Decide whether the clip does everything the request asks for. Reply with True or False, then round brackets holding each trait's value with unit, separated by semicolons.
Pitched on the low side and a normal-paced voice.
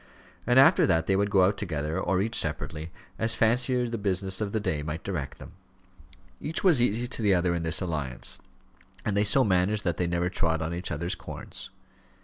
False (95 Hz; 210 wpm)